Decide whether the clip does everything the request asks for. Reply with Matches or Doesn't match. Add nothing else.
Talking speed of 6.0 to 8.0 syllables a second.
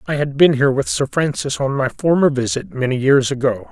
Doesn't match